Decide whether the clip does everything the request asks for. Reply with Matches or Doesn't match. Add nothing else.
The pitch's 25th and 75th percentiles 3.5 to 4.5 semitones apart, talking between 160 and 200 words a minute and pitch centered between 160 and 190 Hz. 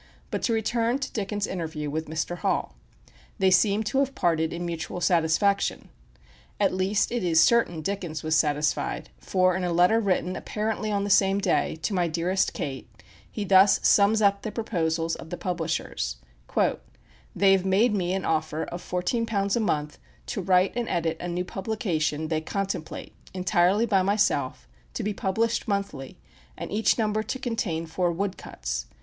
Matches